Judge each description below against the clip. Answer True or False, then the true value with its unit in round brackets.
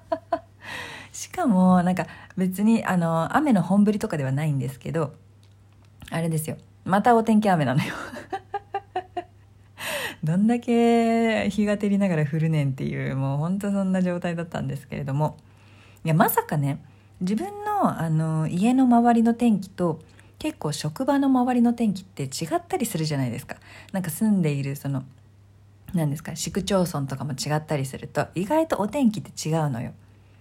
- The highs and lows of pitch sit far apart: True (8.1 semitones)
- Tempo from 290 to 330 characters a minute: True (320 characters per minute)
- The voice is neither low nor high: True (170 Hz)